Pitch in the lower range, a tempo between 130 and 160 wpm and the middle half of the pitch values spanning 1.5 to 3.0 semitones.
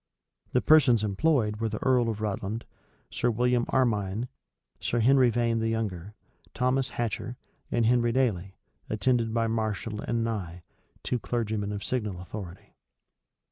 Yes: low, 115 Hz; average, 140 wpm; narrow, 2.6 semitones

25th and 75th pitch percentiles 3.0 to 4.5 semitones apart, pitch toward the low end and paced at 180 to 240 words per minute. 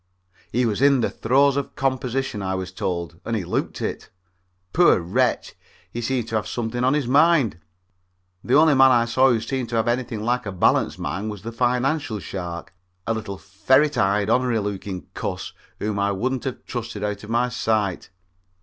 Yes: average, 4.1 semitones; low, 115 Hz; average, 185 wpm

